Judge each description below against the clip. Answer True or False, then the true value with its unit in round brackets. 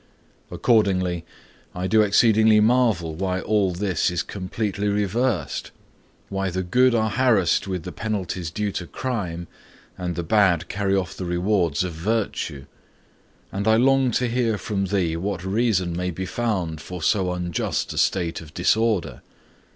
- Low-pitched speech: True (95 Hz)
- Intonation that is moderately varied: True (3.7 semitones)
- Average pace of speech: True (150 wpm)